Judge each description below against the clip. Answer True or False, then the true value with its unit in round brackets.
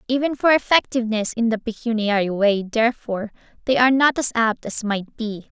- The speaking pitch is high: True (230 Hz)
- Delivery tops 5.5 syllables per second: True (5.7 syllables/s)